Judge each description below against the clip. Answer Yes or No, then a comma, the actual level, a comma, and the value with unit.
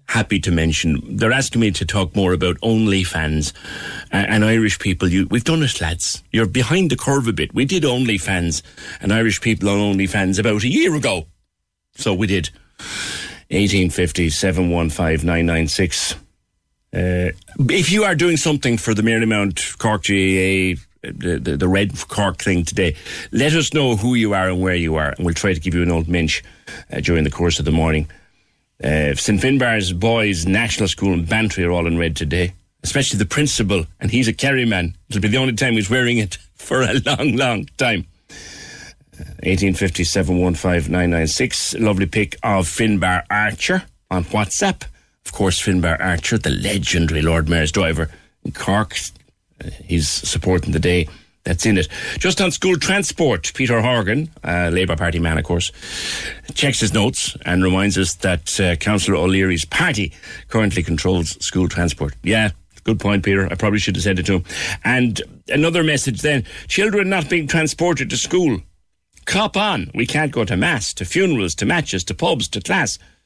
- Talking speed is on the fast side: No, average, 180 wpm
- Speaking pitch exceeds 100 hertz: No, very low, 95 Hz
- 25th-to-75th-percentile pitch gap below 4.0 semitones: No, average, 4.6 semitones